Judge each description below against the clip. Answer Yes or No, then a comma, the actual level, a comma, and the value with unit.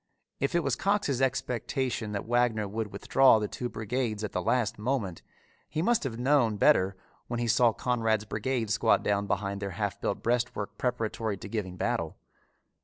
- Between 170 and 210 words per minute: Yes, average, 175 wpm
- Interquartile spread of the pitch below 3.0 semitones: No, average, 3.4 semitones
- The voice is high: No, low, 115 Hz